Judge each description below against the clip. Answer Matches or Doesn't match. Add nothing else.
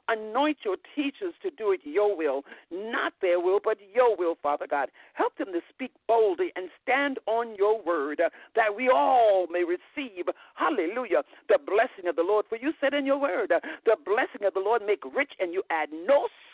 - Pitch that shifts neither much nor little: Doesn't match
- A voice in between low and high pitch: Doesn't match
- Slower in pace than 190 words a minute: Doesn't match